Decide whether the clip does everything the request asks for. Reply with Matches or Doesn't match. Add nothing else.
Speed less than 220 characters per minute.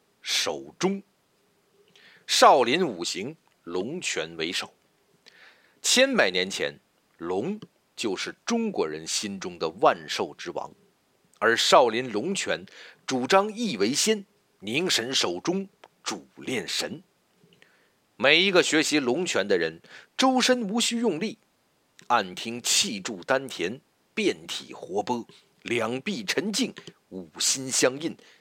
Matches